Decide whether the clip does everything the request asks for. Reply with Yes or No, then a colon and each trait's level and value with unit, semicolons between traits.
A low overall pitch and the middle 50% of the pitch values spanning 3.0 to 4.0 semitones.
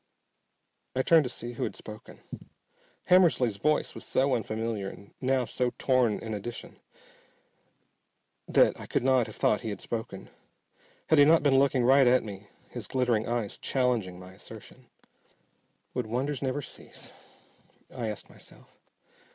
Yes: low, 125 Hz; average, 3.4 semitones